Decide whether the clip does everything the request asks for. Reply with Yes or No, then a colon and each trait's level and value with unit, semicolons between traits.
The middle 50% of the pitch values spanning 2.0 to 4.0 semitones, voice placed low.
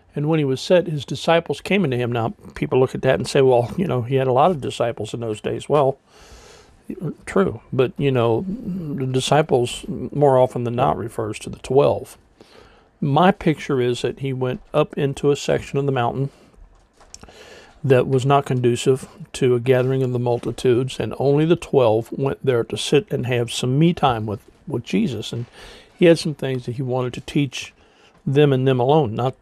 Yes: average, 3.3 semitones; low, 130 Hz